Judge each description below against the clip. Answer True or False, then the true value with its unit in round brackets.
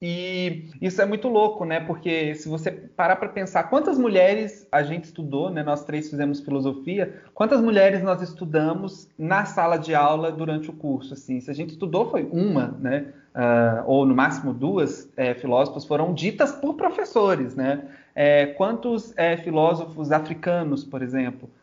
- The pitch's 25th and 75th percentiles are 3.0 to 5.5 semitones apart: True (4.7 semitones)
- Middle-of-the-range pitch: True (160 Hz)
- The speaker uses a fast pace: False (165 wpm)